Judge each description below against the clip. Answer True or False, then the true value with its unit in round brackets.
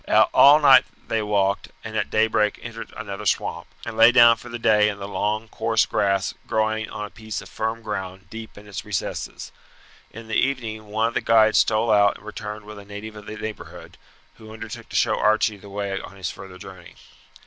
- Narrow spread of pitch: True (1.6 semitones)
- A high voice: False (110 Hz)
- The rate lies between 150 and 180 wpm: False (205 wpm)